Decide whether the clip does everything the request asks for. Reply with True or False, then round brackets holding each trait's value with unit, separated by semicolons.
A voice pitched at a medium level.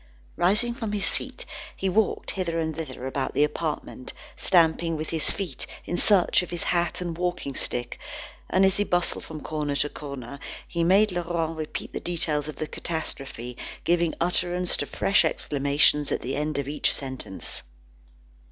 True (165 Hz)